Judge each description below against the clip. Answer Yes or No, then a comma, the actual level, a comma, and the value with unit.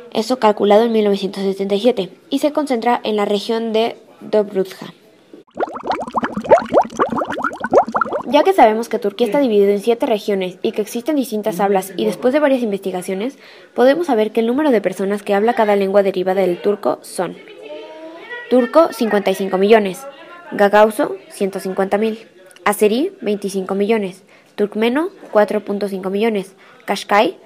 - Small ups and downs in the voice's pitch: No, average, 3.4 semitones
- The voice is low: No, high, 210 Hz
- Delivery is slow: Yes, slow, 130 wpm